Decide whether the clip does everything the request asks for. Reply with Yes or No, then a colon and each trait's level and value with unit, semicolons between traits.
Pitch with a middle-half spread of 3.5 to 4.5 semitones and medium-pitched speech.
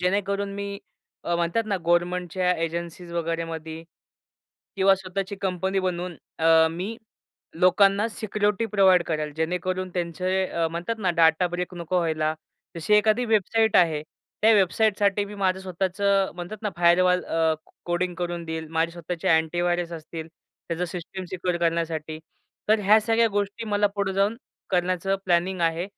No: average, 2.8 semitones; medium, 180 Hz